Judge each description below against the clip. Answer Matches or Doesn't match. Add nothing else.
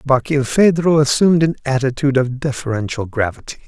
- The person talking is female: Doesn't match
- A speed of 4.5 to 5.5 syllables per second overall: Doesn't match